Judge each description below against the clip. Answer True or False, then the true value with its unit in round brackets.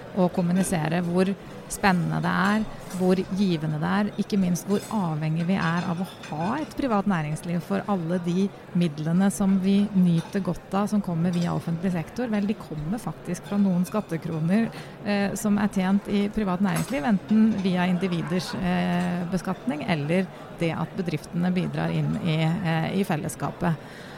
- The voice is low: False (185 Hz)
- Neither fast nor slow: True (160 wpm)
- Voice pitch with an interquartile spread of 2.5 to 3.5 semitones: True (2.9 semitones)